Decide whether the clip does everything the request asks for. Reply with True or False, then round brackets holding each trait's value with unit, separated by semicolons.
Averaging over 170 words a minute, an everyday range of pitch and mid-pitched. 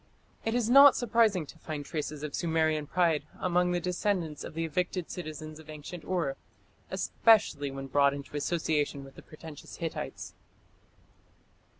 False (150 wpm; 3.4 semitones; 160 Hz)